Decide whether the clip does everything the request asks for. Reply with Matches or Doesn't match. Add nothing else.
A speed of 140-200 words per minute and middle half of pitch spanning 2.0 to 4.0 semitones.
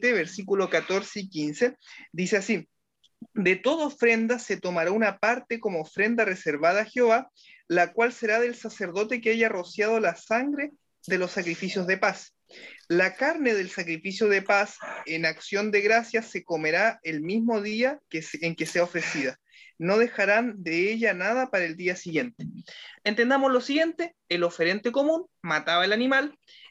Doesn't match